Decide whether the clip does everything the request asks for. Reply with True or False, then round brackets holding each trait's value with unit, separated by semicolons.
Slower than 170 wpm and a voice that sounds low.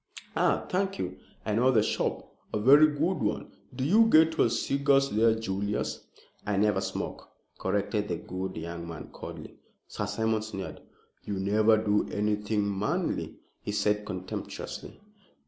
True (145 wpm; 105 Hz)